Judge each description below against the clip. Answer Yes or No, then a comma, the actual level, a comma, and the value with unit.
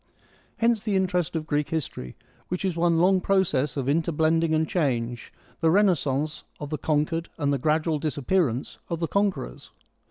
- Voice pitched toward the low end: No, medium, 160 Hz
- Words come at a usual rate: Yes, average, 170 wpm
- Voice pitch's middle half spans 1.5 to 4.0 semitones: Yes, average, 3.5 semitones